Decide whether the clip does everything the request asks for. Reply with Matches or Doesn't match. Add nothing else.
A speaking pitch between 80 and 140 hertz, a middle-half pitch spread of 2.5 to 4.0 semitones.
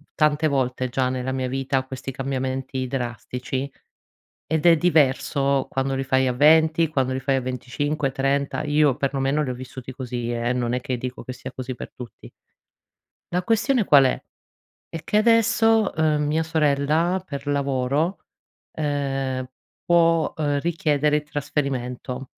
Matches